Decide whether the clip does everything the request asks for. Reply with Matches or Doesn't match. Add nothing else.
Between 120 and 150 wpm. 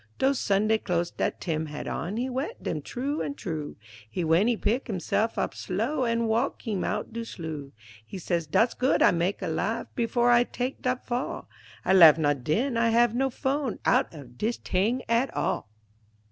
Doesn't match